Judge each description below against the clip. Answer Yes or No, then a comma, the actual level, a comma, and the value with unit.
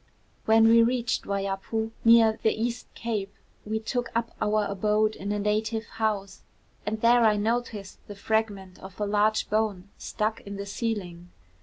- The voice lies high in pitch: Yes, high, 215 Hz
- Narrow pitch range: Yes, narrow, 1.9 semitones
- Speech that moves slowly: No, average, 160 wpm